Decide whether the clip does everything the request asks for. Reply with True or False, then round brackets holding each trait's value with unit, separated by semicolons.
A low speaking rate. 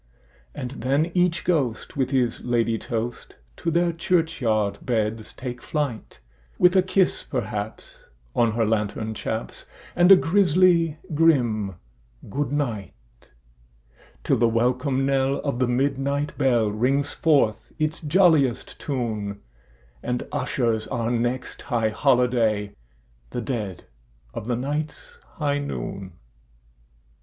True (115 wpm)